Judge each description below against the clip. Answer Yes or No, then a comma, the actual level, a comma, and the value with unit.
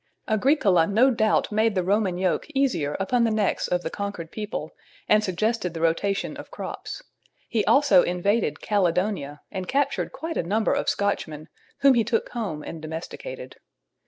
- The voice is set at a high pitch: Yes, high, 200 Hz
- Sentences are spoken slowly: No, average, 160 wpm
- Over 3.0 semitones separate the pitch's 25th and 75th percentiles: Yes, average, 4.4 semitones